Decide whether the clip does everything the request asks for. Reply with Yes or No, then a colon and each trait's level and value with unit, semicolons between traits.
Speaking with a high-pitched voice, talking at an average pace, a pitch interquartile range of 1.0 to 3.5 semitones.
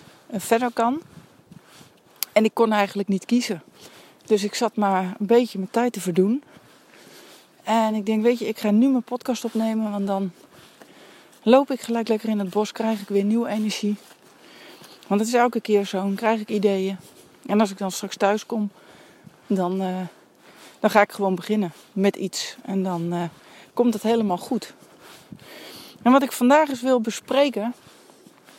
Yes: high, 215 Hz; average, 175 wpm; average, 2.8 semitones